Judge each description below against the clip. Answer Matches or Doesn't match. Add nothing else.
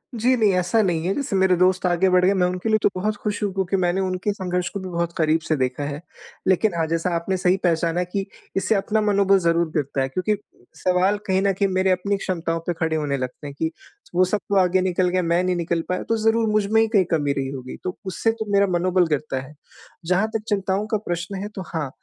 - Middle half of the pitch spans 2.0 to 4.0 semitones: Matches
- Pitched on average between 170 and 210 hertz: Matches